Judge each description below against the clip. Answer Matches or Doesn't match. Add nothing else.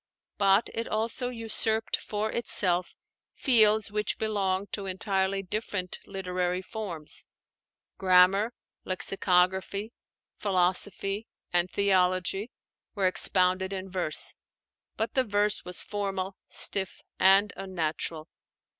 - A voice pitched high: Matches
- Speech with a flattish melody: Matches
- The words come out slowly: Matches